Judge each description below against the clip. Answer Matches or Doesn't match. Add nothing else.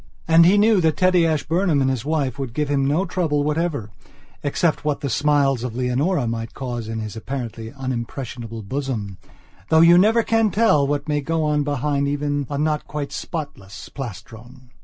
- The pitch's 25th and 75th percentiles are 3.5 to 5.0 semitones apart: Matches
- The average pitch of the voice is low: Doesn't match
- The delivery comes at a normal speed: Matches